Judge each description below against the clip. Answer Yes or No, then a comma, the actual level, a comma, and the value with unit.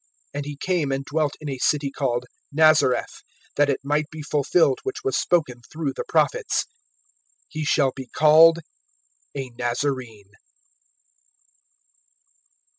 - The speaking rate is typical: No, slow, 125 wpm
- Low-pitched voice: No, medium, 145 Hz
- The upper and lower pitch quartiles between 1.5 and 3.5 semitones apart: Yes, average, 2.9 semitones